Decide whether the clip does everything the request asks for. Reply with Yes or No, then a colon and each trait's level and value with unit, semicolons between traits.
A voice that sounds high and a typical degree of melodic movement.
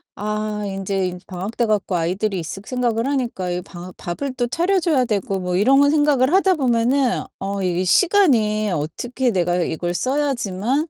No: high, 215 Hz; wide, 6.2 semitones